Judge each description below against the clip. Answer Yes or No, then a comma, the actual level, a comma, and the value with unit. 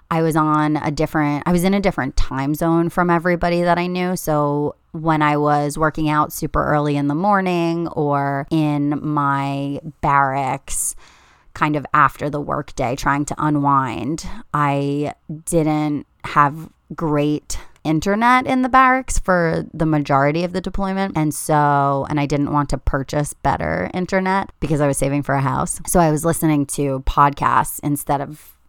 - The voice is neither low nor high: Yes, medium, 150 Hz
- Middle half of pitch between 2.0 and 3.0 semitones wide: Yes, average, 2.7 semitones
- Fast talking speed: No, average, 165 wpm